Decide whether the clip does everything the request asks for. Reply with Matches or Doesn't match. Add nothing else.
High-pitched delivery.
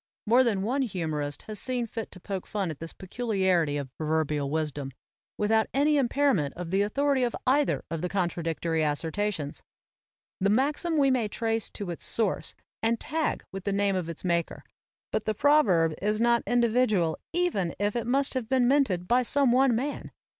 Matches